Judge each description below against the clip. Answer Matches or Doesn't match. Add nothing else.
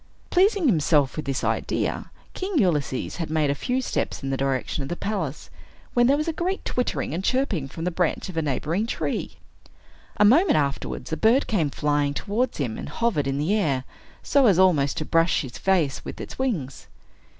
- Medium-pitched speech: Matches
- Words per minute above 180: Matches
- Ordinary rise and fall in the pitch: Doesn't match